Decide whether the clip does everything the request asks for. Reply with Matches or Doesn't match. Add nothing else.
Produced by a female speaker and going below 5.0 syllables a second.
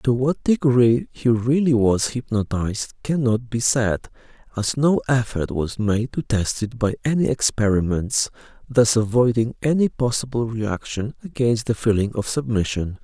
Doesn't match